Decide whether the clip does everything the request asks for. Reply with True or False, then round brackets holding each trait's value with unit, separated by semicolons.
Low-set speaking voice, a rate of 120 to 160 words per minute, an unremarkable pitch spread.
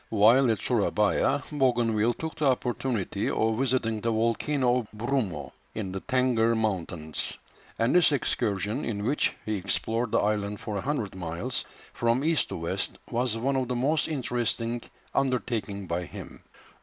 True (115 Hz; 155 wpm; 3.7 semitones)